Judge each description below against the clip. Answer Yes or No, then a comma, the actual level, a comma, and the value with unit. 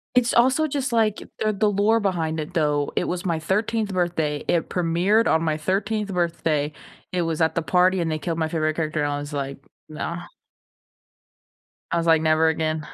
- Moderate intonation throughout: Yes, average, 4.2 semitones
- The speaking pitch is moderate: Yes, medium, 170 Hz